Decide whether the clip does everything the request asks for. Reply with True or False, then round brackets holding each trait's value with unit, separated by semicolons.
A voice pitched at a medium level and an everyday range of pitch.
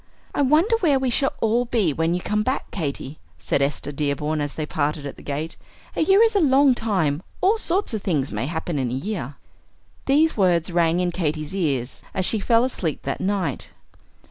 False (180 Hz; 8.8 semitones)